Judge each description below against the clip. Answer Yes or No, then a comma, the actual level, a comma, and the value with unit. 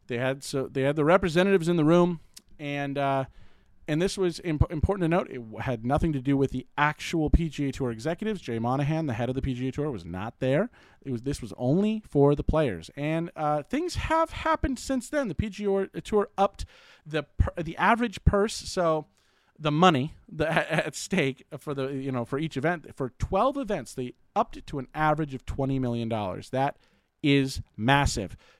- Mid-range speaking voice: Yes, medium, 145 Hz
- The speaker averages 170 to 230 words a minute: Yes, average, 195 wpm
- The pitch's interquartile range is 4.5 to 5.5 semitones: Yes, average, 5.2 semitones